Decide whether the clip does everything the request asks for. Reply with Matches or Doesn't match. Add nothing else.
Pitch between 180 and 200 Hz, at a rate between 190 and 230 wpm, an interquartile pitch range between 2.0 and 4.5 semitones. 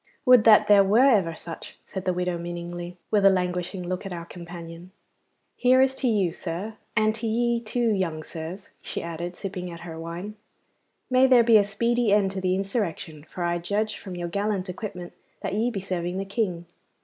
Matches